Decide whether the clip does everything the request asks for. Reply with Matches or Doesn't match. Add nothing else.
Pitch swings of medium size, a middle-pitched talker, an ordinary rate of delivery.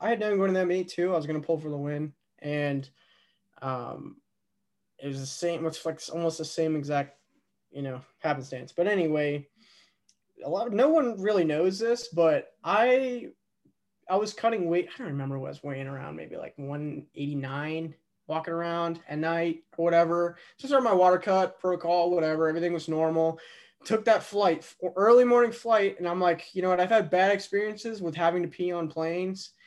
Matches